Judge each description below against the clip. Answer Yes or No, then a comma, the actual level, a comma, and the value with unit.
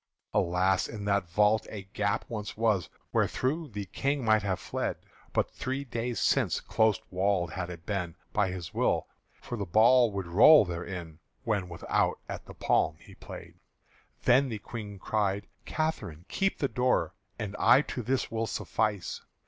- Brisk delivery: No, average, 165 wpm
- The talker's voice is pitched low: Yes, low, 105 Hz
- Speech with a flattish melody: No, average, 4.0 semitones